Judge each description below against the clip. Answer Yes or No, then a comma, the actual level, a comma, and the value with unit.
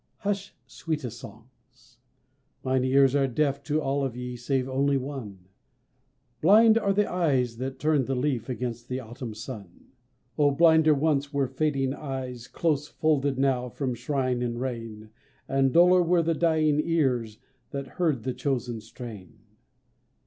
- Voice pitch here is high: No, low, 135 Hz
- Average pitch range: Yes, average, 3.6 semitones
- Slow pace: No, average, 150 wpm